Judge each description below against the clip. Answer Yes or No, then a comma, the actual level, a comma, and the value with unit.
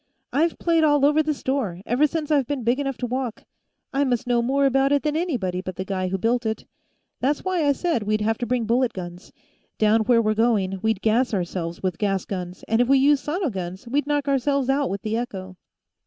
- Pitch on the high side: Yes, high, 245 Hz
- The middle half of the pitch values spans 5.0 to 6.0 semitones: Yes, wide, 5.5 semitones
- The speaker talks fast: Yes, fast, 230 wpm